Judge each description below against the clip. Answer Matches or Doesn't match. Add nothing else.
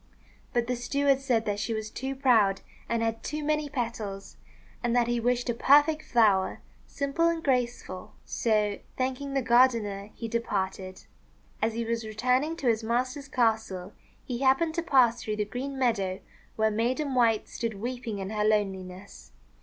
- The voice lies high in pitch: Matches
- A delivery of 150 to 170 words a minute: Matches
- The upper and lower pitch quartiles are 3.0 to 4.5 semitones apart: Matches